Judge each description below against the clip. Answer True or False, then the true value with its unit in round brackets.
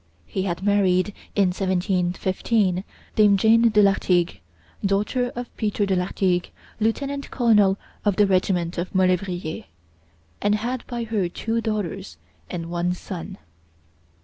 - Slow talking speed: True (125 wpm)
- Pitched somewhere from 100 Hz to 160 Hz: False (195 Hz)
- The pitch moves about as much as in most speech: True (3.1 semitones)